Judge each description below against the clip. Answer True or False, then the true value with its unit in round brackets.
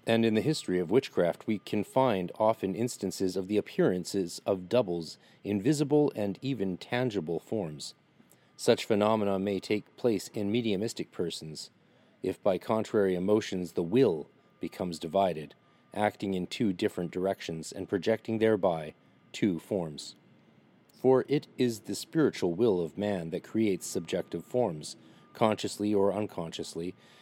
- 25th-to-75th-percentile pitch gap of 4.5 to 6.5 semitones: False (3.3 semitones)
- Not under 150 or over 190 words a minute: False (135 wpm)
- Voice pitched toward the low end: True (105 Hz)